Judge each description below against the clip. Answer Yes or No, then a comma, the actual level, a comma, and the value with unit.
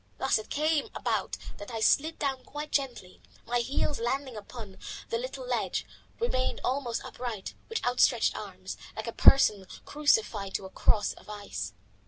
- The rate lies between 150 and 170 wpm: Yes, average, 165 wpm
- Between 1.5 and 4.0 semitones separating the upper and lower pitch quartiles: No, average, 5.2 semitones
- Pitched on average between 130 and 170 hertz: No, high, 245 Hz